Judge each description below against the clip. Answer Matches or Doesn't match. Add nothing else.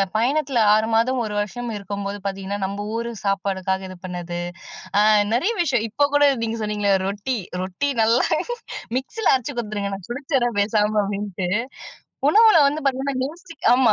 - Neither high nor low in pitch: Doesn't match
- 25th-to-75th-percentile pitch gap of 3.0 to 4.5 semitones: Doesn't match